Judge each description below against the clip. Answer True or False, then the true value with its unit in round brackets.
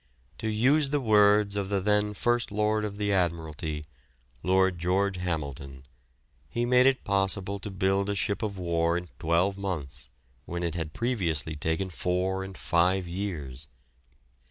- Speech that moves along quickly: False (155 wpm)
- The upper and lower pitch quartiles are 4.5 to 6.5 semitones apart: False (3.4 semitones)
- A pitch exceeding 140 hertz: False (95 Hz)